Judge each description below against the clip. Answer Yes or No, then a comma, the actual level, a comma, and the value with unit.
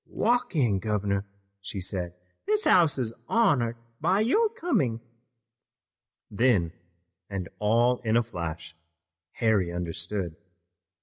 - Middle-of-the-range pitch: No, low, 110 Hz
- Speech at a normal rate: No, slow, 110 wpm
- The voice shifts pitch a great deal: Yes, wide, 7.6 semitones